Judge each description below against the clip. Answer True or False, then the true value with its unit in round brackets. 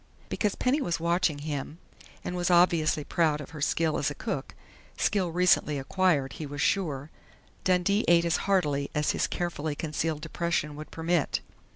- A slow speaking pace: False (165 wpm)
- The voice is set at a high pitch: False (165 Hz)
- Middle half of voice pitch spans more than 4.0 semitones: False (3.0 semitones)